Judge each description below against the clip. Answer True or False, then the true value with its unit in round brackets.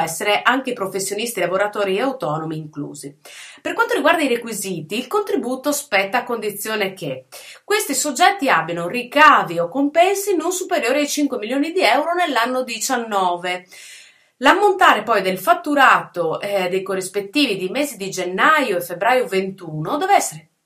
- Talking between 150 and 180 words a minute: False (140 wpm)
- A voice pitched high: True (225 Hz)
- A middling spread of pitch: False (7.8 semitones)